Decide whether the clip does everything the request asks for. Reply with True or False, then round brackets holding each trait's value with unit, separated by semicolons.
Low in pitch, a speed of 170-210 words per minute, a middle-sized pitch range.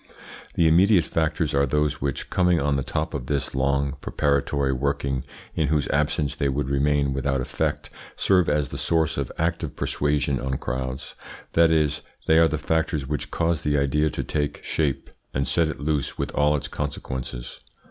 False (75 Hz; 180 wpm; 2.3 semitones)